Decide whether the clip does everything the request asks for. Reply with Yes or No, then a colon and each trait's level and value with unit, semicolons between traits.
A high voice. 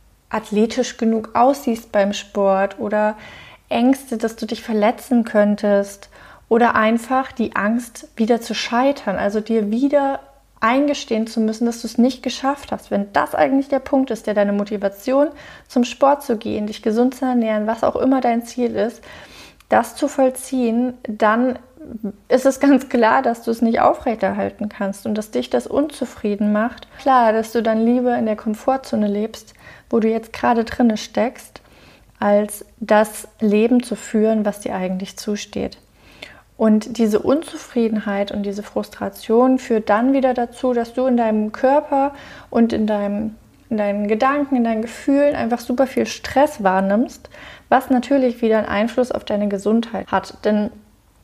Yes: high, 230 Hz